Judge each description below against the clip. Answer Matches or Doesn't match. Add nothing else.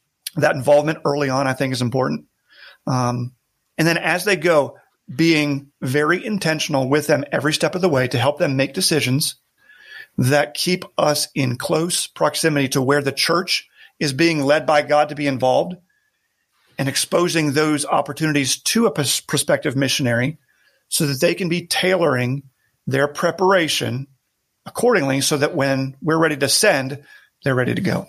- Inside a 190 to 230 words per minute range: Doesn't match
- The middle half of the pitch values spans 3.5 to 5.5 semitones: Doesn't match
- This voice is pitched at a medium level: Matches